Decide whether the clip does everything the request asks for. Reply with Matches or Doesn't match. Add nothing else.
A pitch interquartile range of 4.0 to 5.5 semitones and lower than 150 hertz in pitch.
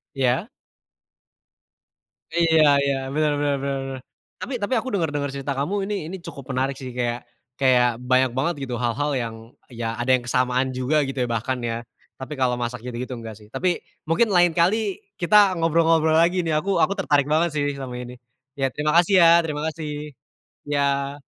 Matches